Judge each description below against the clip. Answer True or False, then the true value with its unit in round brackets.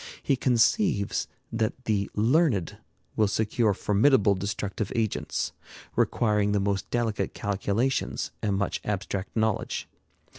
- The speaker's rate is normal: False (110 wpm)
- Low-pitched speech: True (105 Hz)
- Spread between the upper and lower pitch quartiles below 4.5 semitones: True (2.8 semitones)